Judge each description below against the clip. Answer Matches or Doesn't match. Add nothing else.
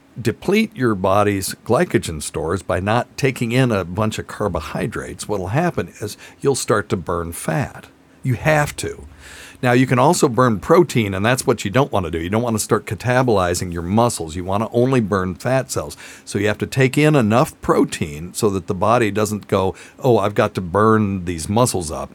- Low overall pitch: Matches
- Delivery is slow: Doesn't match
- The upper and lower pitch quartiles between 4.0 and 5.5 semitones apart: Matches